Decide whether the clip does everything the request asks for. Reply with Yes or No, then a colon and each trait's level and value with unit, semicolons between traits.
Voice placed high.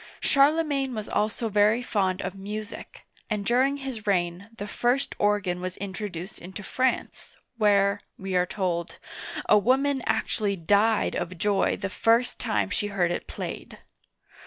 Yes: high, 205 Hz